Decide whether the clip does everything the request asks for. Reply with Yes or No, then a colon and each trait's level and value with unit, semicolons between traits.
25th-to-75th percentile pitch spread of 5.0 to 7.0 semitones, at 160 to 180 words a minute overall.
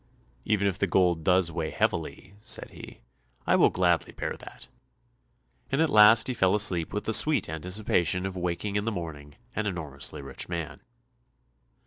No: average, 4.0 semitones; average, 165 wpm